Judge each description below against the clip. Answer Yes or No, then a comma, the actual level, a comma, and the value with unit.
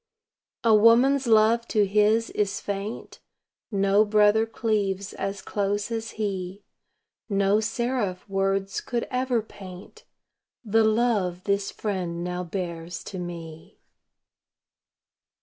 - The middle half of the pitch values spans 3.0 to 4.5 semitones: No, narrow, 2.5 semitones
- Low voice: No, high, 205 Hz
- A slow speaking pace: Yes, slow, 110 wpm